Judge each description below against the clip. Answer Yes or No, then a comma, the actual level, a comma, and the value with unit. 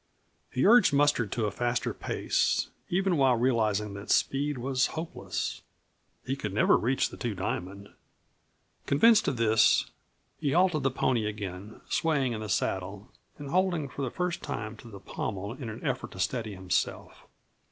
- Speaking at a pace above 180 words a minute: No, average, 165 wpm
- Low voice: Yes, low, 120 Hz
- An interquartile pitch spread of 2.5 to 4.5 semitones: No, average, 5.2 semitones